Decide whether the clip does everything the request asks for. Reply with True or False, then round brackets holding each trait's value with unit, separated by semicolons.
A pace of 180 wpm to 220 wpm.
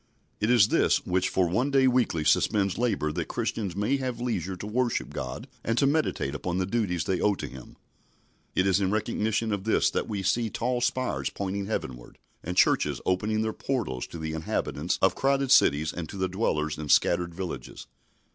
True (195 wpm)